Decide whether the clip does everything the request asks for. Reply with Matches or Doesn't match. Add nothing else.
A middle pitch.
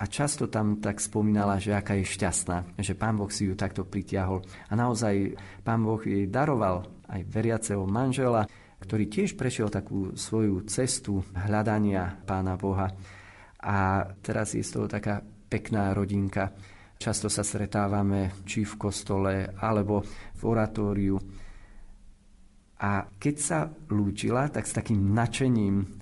Doesn't match